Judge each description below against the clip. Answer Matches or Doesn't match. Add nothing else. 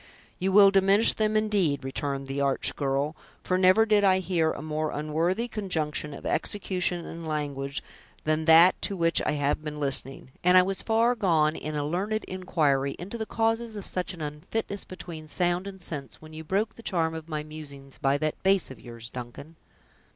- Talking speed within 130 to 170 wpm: Doesn't match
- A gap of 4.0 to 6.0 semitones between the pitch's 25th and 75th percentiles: Matches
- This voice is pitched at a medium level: Matches